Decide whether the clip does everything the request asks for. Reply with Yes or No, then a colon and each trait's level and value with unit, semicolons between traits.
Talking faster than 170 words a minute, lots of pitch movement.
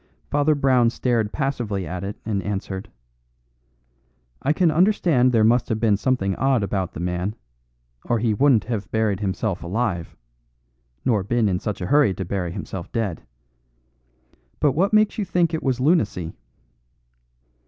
No: average, 155 wpm; wide, 5.7 semitones